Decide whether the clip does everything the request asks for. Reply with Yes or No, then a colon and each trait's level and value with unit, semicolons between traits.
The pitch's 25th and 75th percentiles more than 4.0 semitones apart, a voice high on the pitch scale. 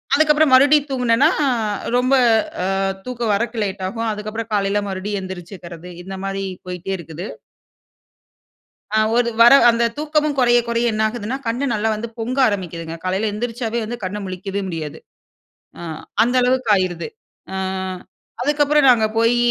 Yes: average, 4.4 semitones; high, 225 Hz